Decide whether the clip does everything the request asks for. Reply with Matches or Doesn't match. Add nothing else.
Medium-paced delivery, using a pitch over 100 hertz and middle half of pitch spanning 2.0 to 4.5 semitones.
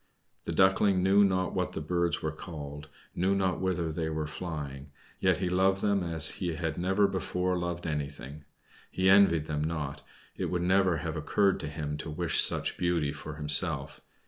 Doesn't match